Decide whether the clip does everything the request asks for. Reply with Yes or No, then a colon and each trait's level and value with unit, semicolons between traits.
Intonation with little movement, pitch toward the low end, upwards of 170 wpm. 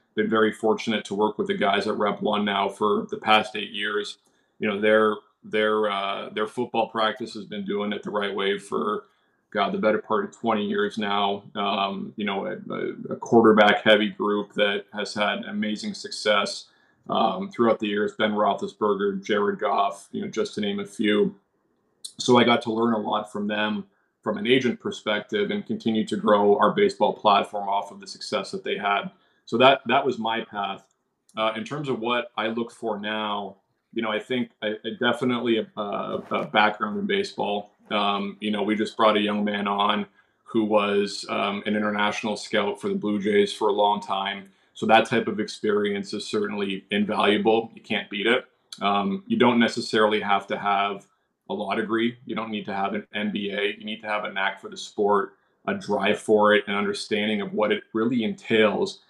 Yes: narrow, 1.6 semitones; low, 105 Hz; average, 200 wpm